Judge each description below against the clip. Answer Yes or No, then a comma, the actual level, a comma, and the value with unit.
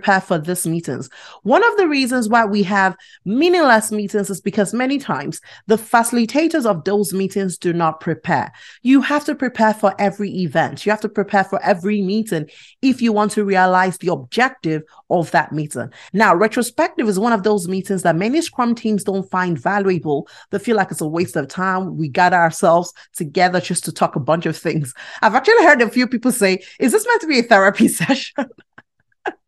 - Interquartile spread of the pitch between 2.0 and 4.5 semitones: No, average, 5.1 semitones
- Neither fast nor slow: Yes, average, 195 wpm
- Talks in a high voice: Yes, high, 200 Hz